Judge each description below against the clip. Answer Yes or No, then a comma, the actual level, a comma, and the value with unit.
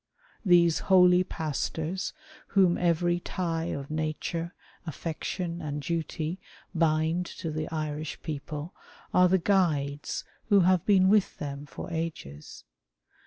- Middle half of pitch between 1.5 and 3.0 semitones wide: Yes, narrow, 2.6 semitones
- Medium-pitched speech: Yes, medium, 165 Hz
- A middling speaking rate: No, slow, 120 wpm